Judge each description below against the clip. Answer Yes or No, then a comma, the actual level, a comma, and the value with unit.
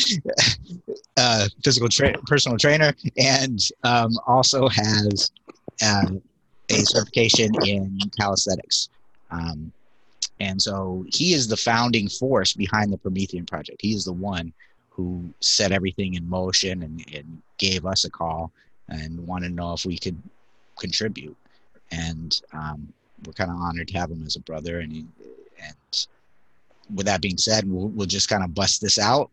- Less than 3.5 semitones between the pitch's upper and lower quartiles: No, average, 4.3 semitones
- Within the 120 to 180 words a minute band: Yes, average, 155 wpm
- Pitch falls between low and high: No, very low, 95 Hz